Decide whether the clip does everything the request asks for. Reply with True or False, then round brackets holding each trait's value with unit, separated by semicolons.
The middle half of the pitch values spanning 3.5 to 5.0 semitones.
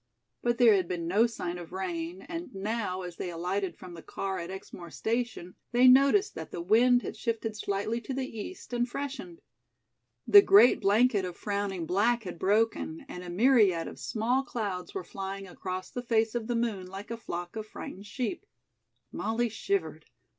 True (4.6 semitones)